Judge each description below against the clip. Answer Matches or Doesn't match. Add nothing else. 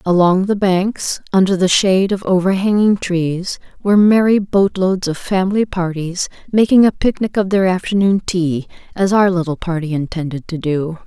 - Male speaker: Doesn't match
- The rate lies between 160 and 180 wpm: Matches